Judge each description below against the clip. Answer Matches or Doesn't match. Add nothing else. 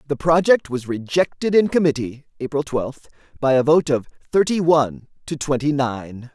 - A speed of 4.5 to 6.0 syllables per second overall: Matches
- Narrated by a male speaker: Matches